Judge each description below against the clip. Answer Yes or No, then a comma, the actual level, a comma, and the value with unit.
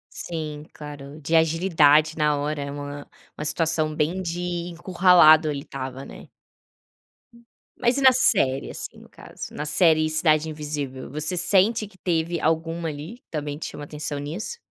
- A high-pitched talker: No, medium, 155 Hz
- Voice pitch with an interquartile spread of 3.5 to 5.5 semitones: No, narrow, 2.5 semitones